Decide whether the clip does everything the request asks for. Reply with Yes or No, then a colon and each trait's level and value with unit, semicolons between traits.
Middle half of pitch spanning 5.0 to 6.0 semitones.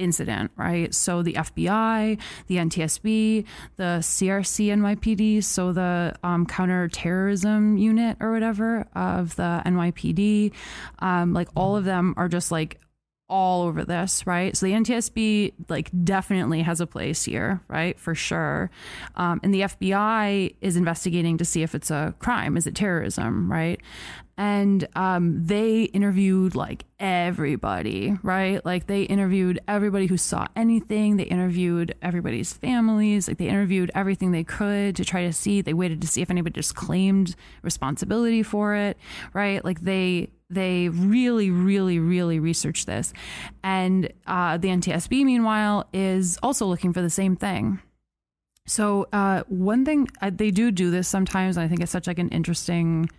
No: average, 2.7 semitones